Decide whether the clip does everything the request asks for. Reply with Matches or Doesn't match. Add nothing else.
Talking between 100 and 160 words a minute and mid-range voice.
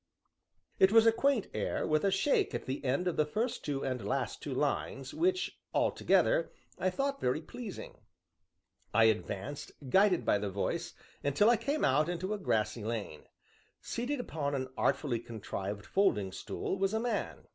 Doesn't match